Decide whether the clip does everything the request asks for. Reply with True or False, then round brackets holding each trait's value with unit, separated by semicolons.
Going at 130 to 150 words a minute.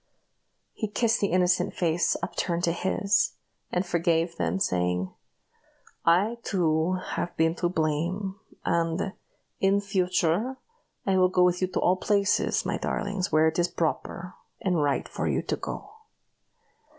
True (145 wpm)